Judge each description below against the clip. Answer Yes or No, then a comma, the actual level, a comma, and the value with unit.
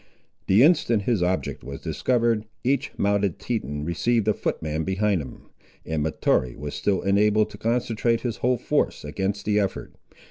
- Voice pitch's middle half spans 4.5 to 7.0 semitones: Yes, average, 5.1 semitones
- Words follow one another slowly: No, average, 155 wpm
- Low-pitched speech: Yes, low, 100 Hz